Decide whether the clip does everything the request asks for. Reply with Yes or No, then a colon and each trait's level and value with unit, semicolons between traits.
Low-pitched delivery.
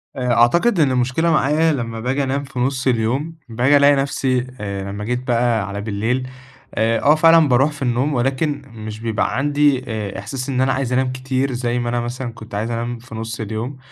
Yes: low, 125 Hz